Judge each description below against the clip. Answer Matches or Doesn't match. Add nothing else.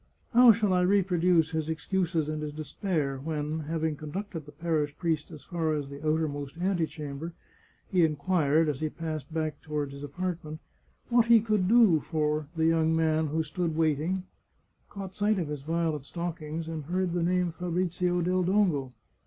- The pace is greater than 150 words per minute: Matches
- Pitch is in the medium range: Matches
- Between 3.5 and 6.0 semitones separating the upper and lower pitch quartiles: Doesn't match